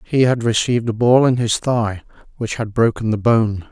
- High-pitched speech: No, low, 115 Hz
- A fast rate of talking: Yes, fast, 210 wpm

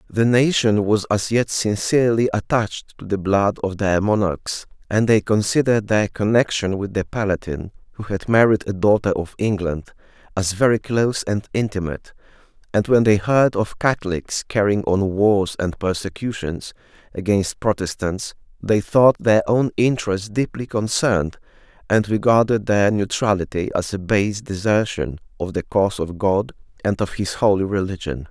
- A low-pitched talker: Yes, low, 100 Hz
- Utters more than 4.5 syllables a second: Yes, 4.9 syllables/s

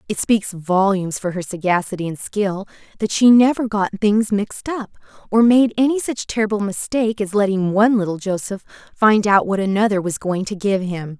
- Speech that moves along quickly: No, average, 190 wpm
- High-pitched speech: Yes, high, 205 Hz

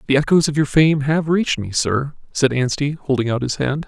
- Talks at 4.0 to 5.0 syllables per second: No, 5.4 syllables/s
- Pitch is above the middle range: No, medium, 140 Hz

